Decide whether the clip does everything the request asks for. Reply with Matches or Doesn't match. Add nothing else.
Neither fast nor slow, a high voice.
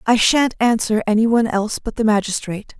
Matches